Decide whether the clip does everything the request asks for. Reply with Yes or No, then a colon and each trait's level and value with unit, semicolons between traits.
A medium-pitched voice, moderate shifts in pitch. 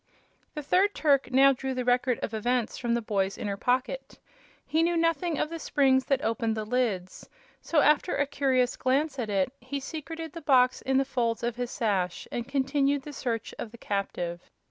No: very high, 255 Hz; average, 3.8 semitones